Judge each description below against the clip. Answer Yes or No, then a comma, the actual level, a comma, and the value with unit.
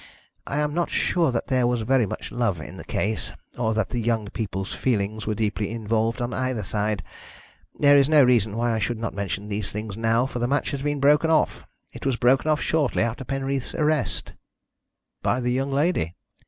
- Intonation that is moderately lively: Yes, average, 4.0 semitones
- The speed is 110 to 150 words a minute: No, fast, 205 wpm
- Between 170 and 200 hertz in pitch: No, low, 120 Hz